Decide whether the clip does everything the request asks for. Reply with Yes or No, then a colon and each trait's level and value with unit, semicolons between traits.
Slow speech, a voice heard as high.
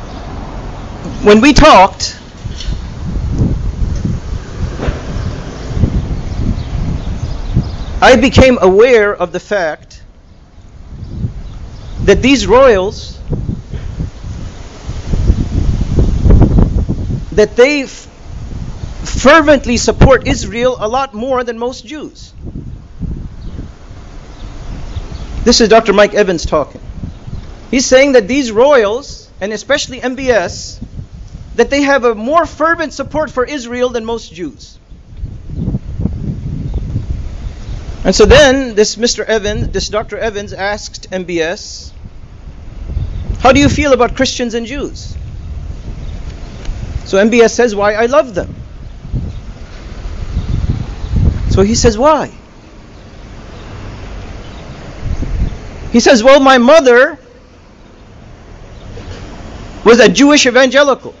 Yes: slow, 85 wpm; high, 210 Hz